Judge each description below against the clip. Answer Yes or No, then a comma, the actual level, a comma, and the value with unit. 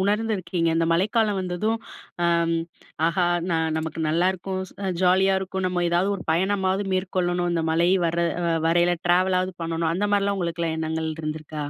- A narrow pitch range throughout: Yes, narrow, 2.3 semitones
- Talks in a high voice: No, medium, 175 Hz